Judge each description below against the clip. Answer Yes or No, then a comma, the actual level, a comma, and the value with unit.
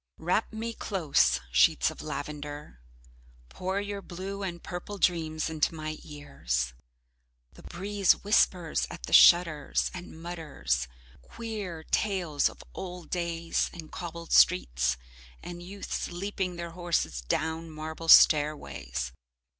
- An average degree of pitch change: Yes, average, 3.5 semitones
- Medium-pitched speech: Yes, medium, 165 Hz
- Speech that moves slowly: Yes, slow, 120 wpm